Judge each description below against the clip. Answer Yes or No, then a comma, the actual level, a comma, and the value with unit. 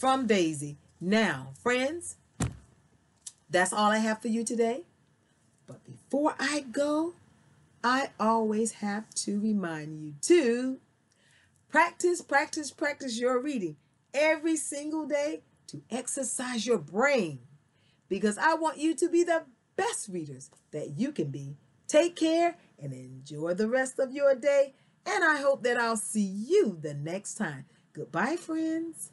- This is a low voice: No, high, 240 Hz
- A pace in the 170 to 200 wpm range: No, average, 140 wpm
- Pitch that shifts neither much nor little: No, wide, 8.6 semitones